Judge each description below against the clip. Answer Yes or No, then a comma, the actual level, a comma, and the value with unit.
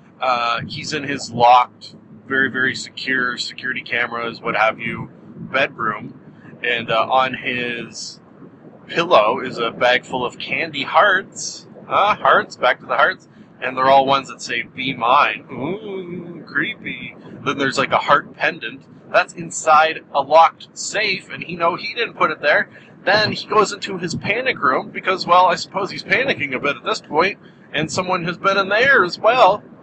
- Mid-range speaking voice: Yes, medium, 155 Hz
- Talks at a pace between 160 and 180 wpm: Yes, average, 175 wpm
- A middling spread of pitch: No, wide, 6.7 semitones